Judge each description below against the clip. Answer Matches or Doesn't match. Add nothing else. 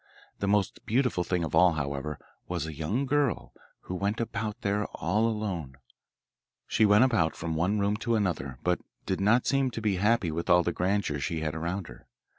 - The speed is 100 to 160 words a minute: Doesn't match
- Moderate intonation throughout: Matches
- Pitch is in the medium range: Doesn't match